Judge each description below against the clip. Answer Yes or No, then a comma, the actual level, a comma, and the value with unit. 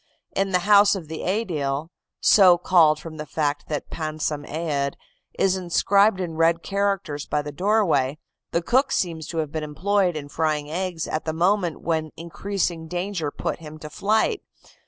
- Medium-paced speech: Yes, average, 170 wpm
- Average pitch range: Yes, average, 3.9 semitones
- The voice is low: No, medium, 165 Hz